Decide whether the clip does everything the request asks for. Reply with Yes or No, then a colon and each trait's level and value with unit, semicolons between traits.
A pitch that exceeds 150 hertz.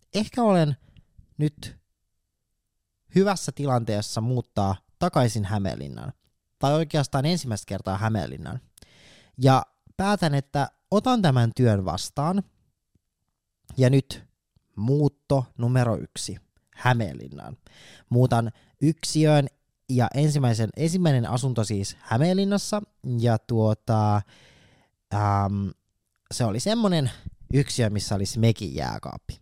No: low, 120 Hz